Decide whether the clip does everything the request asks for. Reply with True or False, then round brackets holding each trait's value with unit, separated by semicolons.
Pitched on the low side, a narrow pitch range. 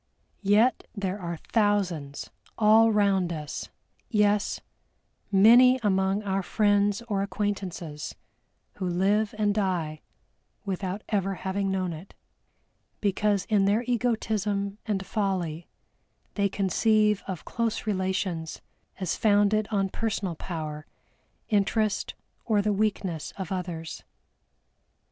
False (200 Hz; 2.3 semitones)